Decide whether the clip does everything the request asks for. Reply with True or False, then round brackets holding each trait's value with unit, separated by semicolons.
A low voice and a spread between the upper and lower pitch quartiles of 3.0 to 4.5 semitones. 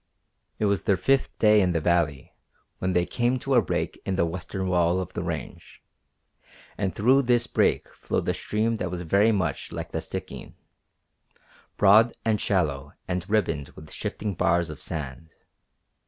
True (95 Hz; 4.2 semitones)